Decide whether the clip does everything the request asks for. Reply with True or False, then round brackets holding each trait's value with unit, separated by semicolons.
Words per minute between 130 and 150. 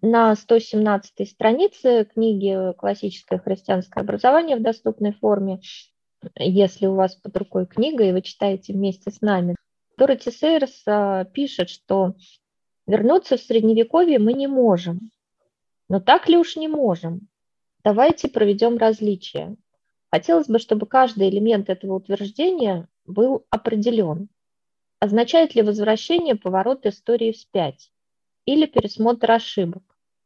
False (115 wpm)